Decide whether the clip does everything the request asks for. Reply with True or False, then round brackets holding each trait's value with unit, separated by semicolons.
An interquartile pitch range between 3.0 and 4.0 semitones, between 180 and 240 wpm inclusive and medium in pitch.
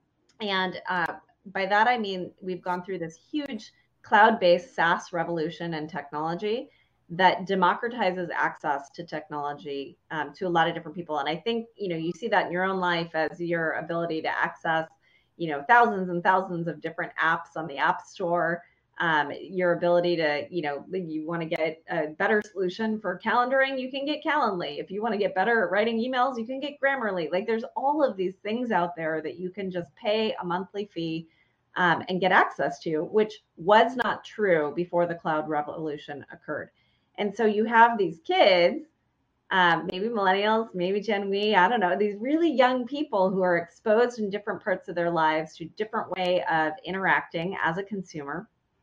False (4.4 semitones; 190 wpm; 180 Hz)